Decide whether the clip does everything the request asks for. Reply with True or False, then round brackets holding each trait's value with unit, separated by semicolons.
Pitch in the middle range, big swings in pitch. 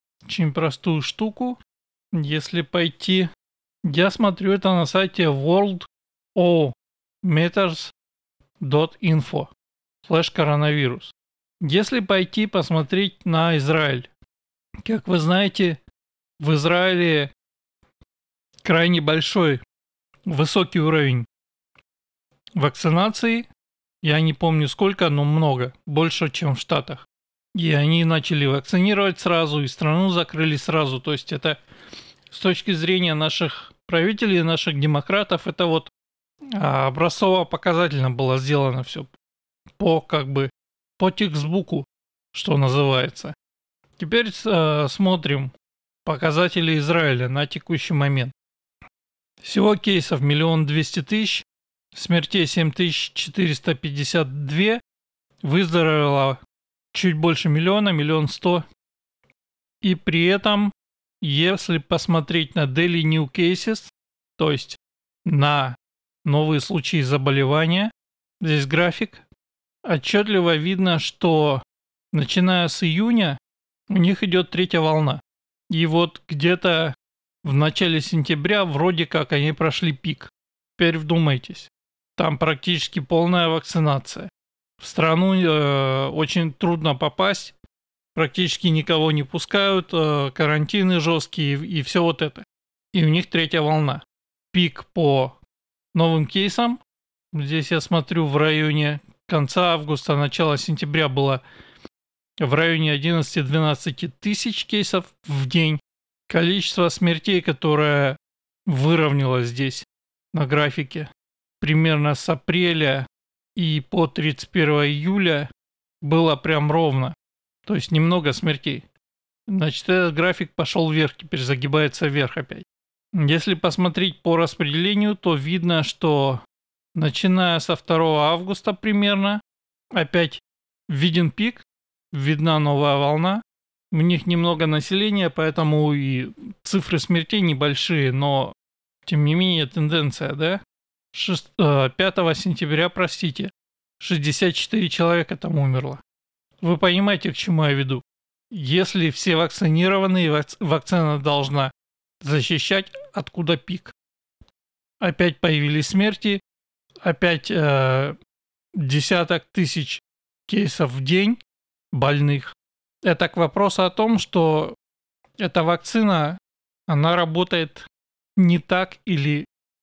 False (160 Hz; 3.9 semitones)